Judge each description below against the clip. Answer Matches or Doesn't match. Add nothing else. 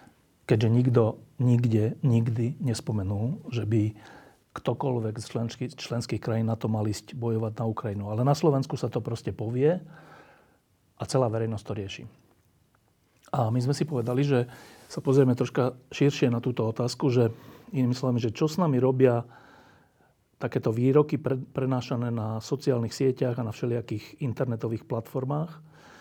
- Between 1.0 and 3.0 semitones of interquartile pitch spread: Matches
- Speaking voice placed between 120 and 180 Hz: Matches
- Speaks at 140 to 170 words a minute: Matches